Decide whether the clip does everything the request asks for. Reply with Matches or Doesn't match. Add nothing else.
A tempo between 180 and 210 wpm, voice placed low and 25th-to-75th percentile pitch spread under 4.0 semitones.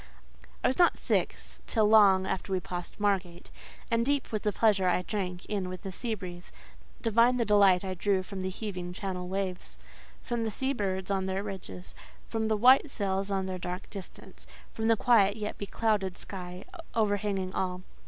Doesn't match